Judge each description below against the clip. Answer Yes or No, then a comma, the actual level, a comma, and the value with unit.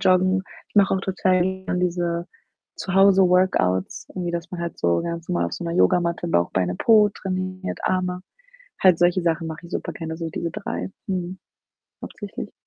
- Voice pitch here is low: No, medium, 180 Hz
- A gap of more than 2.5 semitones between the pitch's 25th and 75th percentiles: No, narrow, 1.9 semitones